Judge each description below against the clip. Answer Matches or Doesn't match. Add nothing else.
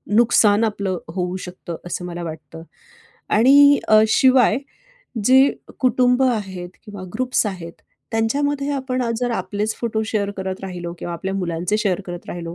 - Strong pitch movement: Matches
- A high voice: Matches